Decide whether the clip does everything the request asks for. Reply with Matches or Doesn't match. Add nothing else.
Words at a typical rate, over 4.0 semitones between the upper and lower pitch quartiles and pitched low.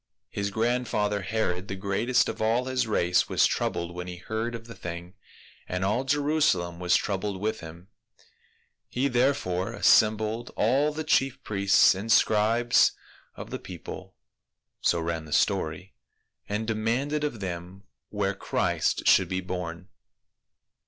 Matches